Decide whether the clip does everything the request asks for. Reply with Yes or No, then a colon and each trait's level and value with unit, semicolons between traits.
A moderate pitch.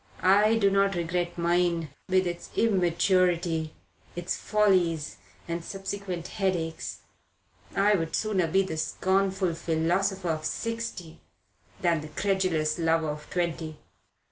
Yes: medium, 175 Hz